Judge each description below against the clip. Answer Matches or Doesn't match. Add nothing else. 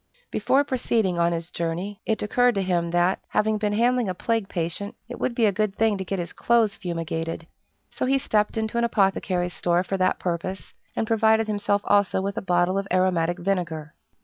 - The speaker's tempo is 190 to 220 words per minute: Matches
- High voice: Matches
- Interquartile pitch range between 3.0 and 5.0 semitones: Matches